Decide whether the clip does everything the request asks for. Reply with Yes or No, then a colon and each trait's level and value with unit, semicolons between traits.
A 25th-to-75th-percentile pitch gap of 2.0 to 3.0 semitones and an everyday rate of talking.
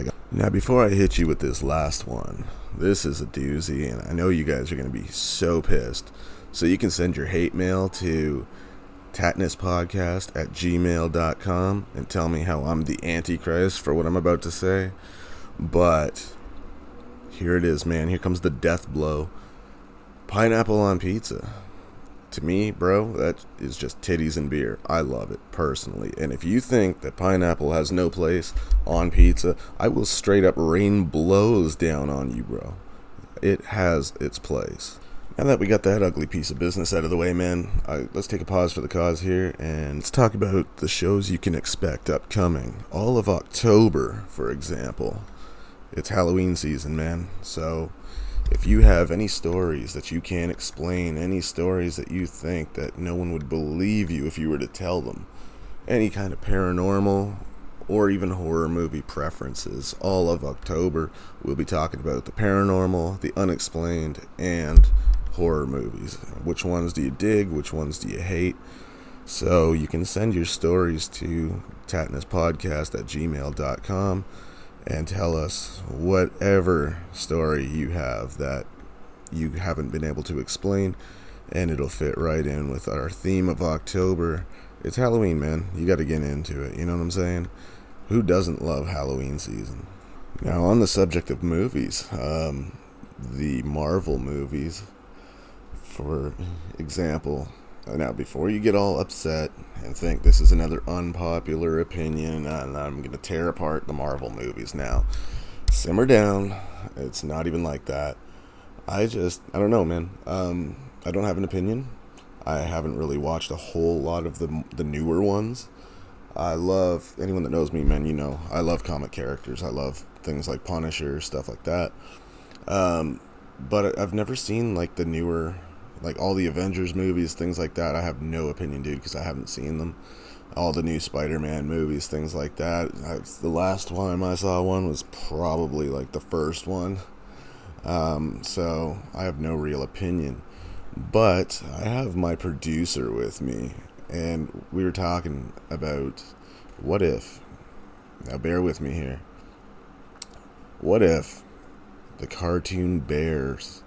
No: average, 3.5 semitones; average, 165 wpm